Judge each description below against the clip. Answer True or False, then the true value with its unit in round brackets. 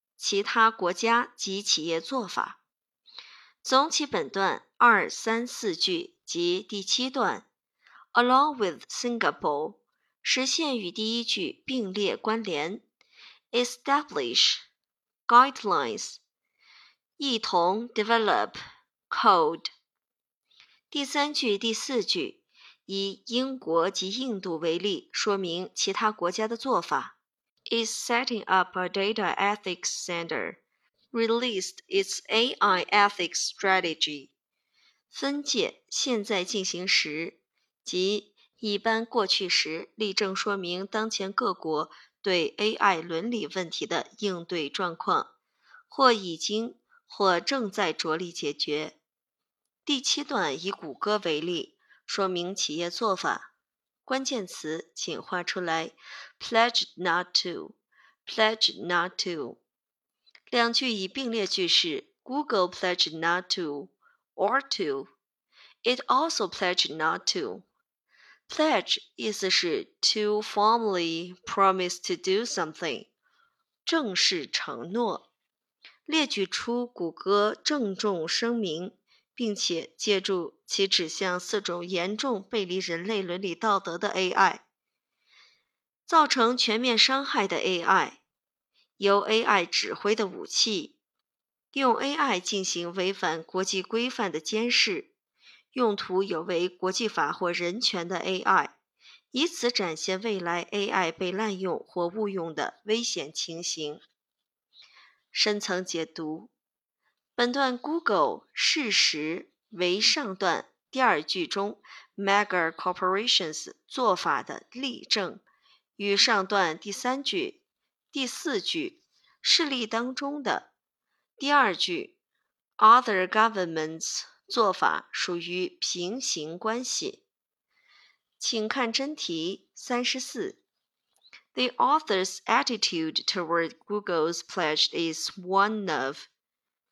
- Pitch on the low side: False (210 Hz)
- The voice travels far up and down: True (5.9 semitones)